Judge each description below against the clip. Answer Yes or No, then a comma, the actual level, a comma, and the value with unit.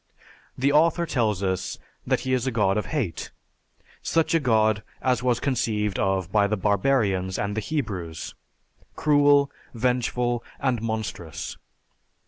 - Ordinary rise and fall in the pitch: Yes, average, 4.6 semitones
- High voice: No, low, 115 Hz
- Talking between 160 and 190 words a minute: No, slow, 135 wpm